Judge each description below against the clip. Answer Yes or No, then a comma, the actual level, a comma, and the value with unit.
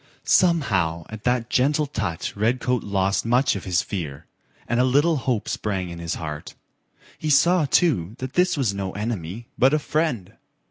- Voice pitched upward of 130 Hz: No, low, 115 Hz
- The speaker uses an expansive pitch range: Yes, wide, 6.4 semitones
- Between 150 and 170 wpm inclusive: Yes, average, 165 wpm